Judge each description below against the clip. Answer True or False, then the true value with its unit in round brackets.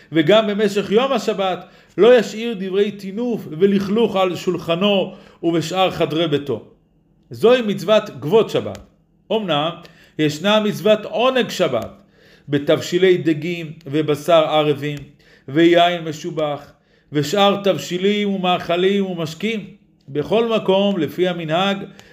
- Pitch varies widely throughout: False (4.0 semitones)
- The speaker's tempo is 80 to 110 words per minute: True (100 wpm)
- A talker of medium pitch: True (180 Hz)